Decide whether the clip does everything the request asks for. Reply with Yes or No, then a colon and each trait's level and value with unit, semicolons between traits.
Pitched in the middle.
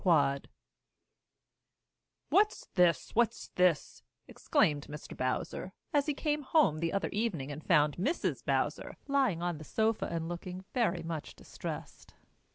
Yes: medium, 175 Hz